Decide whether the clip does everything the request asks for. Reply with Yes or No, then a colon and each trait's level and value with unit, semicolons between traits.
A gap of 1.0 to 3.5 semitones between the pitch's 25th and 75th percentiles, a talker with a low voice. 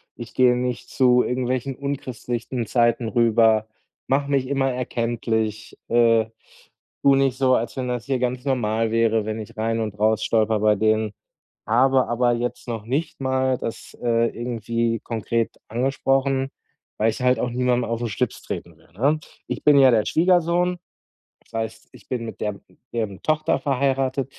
Yes: average, 2.7 semitones; low, 120 Hz